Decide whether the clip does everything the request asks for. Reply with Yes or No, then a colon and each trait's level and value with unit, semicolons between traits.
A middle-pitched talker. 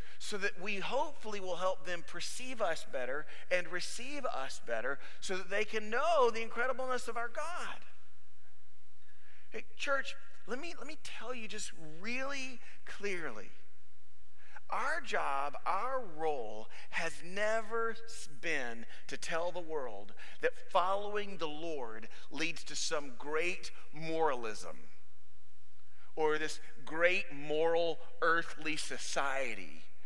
Yes: medium, 175 Hz